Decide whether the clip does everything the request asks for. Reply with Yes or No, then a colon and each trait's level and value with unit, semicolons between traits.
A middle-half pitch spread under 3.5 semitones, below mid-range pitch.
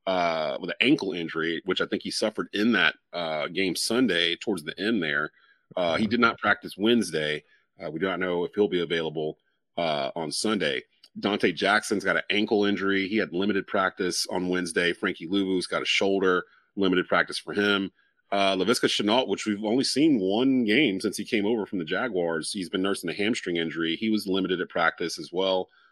Yes: average, 2.7 semitones; very low, 95 Hz